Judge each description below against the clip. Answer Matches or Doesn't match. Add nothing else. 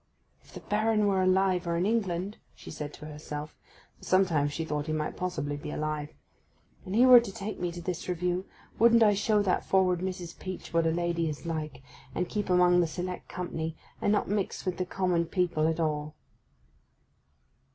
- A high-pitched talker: Doesn't match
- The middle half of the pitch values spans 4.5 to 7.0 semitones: Doesn't match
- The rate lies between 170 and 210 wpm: Matches